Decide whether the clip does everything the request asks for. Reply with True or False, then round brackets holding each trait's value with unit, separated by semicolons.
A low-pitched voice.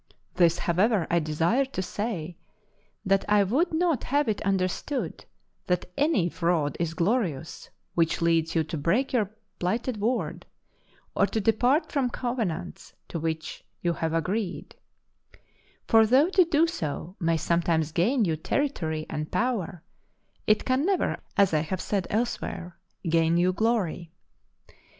False (185 Hz)